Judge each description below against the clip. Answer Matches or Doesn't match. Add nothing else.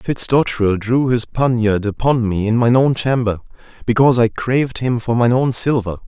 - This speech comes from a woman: Doesn't match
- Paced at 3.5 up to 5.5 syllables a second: Matches